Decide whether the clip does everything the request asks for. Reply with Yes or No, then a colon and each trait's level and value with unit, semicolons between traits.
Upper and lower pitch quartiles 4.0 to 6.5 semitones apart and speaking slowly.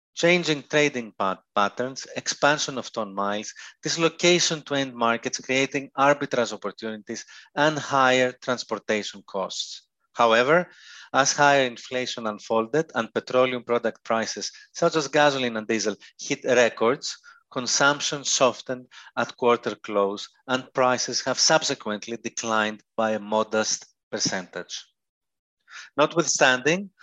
Yes: average, 4.5 semitones; slow, 110 wpm